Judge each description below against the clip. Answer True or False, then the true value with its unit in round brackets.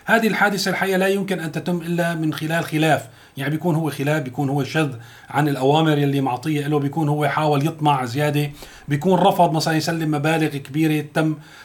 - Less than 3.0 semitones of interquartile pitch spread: True (2.4 semitones)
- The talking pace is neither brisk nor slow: False (180 wpm)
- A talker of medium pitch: True (155 Hz)